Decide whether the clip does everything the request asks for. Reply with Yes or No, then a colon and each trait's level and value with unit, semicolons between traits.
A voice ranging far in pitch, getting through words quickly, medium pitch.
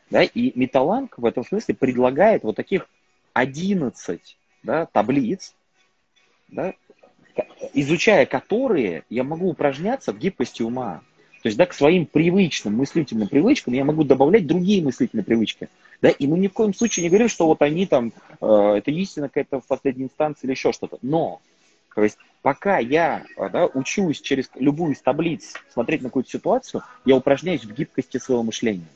Yes: wide, 6.3 semitones; fast, 165 wpm; medium, 145 Hz